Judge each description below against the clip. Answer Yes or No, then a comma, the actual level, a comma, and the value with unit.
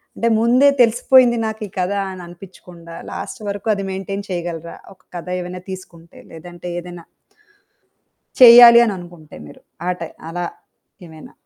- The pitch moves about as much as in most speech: Yes, average, 4.2 semitones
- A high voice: No, medium, 180 Hz